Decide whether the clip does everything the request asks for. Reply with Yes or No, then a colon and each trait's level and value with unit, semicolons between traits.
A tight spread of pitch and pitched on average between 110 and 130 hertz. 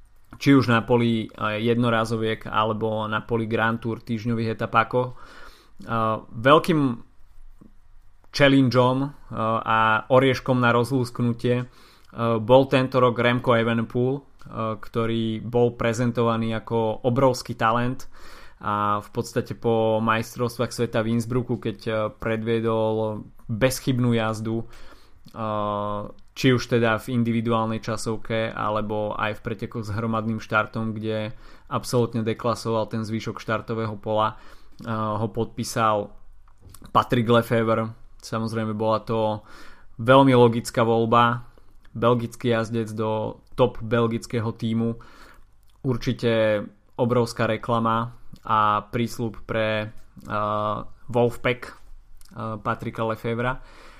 Yes: narrow, 1.6 semitones; low, 115 Hz